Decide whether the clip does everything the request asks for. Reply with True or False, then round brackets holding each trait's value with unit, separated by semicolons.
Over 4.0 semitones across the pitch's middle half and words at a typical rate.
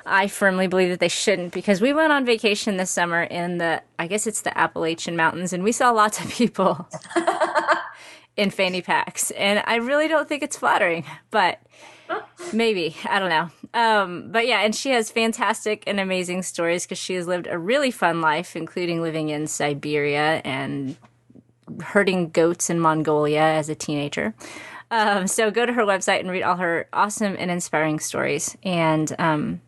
True (4.9 semitones; 180 wpm)